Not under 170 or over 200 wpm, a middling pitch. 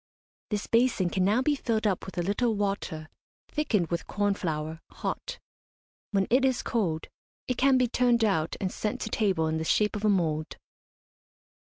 No: average, 180 wpm; high, 205 Hz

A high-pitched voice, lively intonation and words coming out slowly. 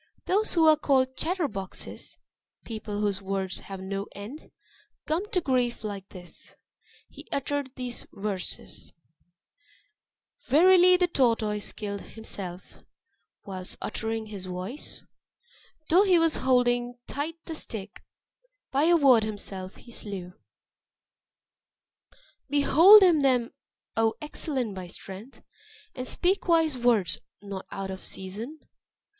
Yes: high, 240 Hz; wide, 7.3 semitones; slow, 120 wpm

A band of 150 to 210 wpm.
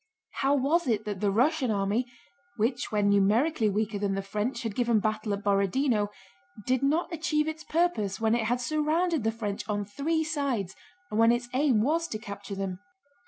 Yes: average, 185 wpm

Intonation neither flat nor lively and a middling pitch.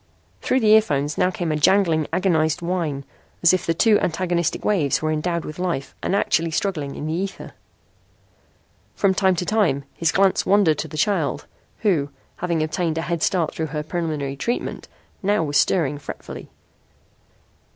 Yes: average, 3.5 semitones; medium, 170 Hz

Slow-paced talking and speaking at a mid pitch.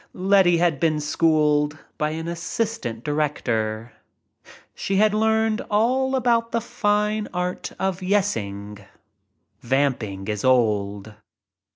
Yes: slow, 110 wpm; medium, 165 Hz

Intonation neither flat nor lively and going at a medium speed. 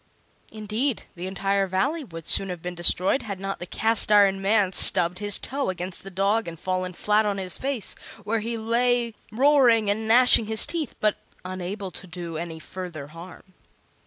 Yes: average, 3.5 semitones; average, 180 wpm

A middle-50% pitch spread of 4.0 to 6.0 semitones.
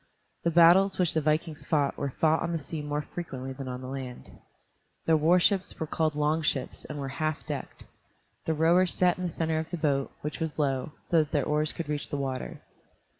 No: narrow, 2.5 semitones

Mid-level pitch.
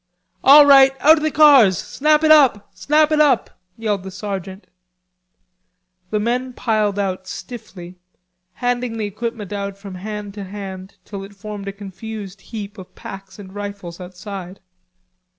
No: high, 205 Hz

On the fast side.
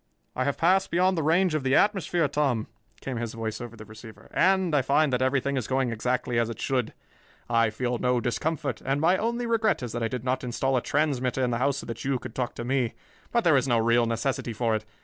Yes: fast, 245 wpm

